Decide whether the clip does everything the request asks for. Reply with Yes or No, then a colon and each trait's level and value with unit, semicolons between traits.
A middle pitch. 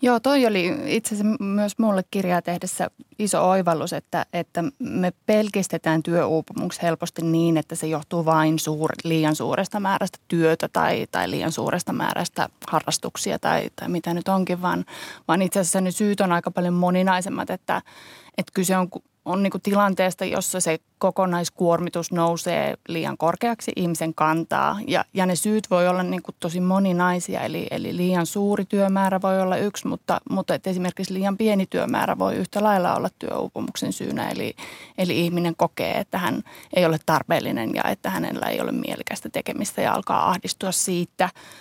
Yes: medium, 180 Hz